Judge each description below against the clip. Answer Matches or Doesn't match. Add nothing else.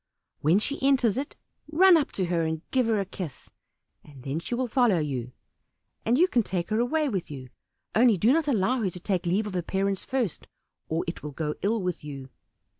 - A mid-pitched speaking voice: Doesn't match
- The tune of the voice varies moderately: Doesn't match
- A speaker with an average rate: Doesn't match